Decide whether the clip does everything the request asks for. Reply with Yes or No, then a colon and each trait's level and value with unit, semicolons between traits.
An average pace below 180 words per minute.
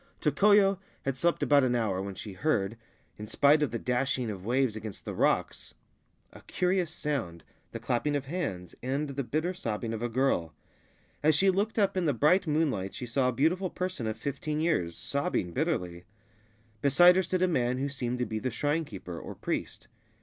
No: average, 195 wpm